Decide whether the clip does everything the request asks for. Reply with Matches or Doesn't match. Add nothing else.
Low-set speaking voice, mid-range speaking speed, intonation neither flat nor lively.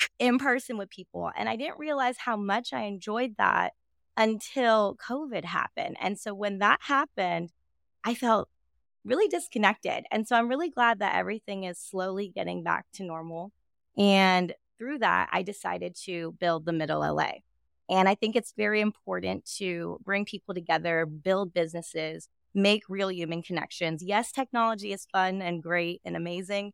Doesn't match